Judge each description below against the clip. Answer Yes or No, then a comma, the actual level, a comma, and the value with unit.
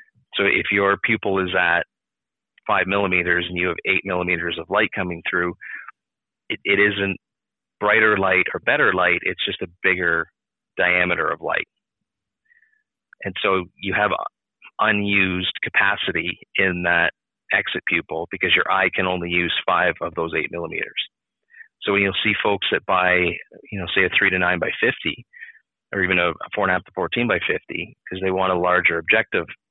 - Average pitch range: No, narrow, 2.1 semitones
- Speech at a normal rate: Yes, average, 175 wpm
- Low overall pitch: Yes, very low, 95 Hz